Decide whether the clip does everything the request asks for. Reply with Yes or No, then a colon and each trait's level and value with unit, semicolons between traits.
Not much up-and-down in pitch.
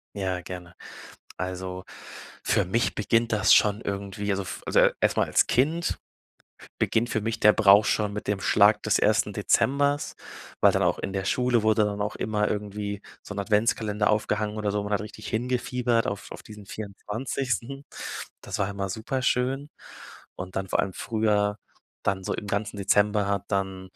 Yes: narrow, 1.9 semitones